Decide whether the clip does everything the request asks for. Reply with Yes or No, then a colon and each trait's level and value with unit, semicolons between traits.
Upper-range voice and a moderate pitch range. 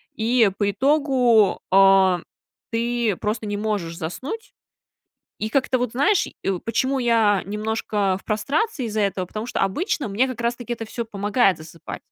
Yes: high, 220 Hz; average, 3.8 semitones